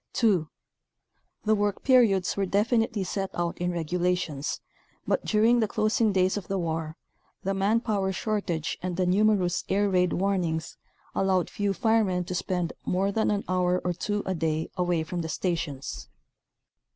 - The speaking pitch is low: No, medium, 185 Hz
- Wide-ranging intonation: No, average, 2.8 semitones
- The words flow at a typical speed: Yes, average, 165 wpm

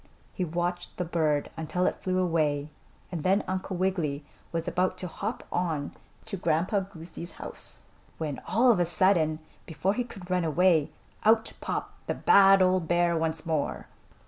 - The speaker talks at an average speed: Yes, average, 165 wpm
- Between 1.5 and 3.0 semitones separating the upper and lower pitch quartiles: Yes, average, 2.7 semitones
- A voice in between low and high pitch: Yes, medium, 175 Hz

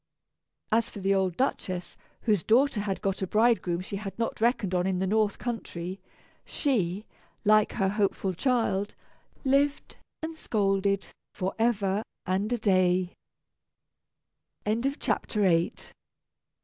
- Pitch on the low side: No, high, 200 Hz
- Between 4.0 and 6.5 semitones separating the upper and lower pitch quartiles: No, average, 3.3 semitones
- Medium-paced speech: No, slow, 115 wpm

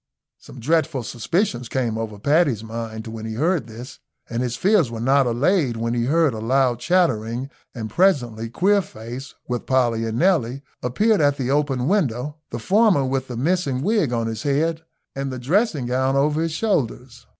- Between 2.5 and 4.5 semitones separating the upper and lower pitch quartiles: No, average, 5.2 semitones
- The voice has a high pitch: No, low, 130 Hz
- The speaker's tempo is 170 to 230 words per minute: Yes, average, 175 wpm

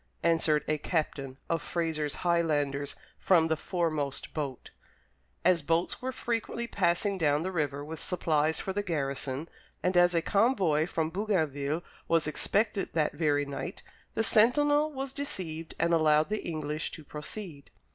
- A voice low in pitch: No, medium, 165 Hz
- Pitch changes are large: No, average, 3.9 semitones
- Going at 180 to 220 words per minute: No, average, 150 wpm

